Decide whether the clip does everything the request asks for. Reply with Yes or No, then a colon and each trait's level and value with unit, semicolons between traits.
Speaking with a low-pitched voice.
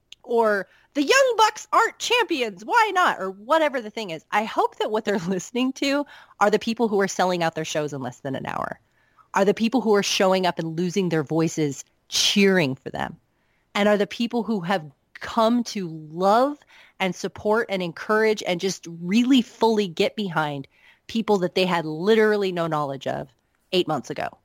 No: high, 200 Hz